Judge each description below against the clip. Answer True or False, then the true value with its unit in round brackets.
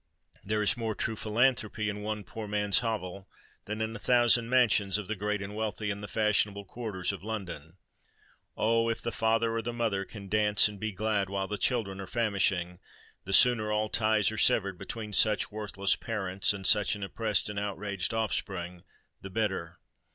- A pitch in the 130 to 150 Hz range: False (105 Hz)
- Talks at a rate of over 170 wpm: True (185 wpm)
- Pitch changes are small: True (2.2 semitones)